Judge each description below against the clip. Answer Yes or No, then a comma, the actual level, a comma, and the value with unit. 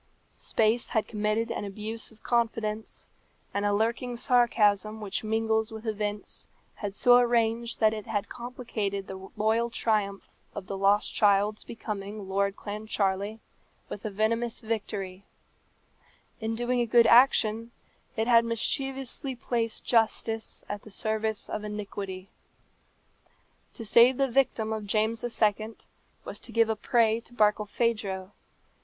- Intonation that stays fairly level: Yes, narrow, 2.0 semitones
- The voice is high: Yes, high, 220 Hz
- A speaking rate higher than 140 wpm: No, slow, 135 wpm